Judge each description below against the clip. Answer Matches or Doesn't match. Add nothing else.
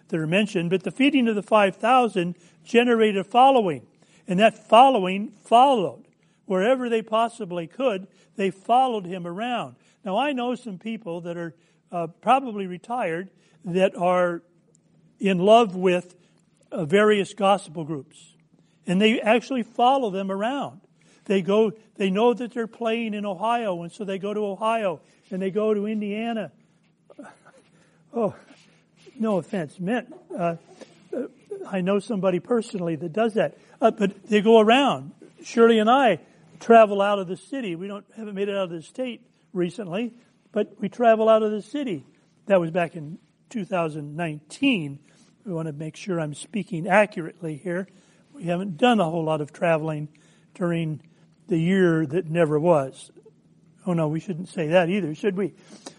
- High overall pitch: Matches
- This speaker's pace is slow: Doesn't match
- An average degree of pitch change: Matches